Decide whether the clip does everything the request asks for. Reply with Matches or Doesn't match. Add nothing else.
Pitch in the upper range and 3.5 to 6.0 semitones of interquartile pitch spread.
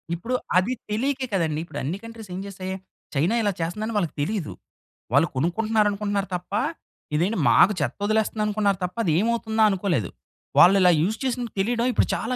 Matches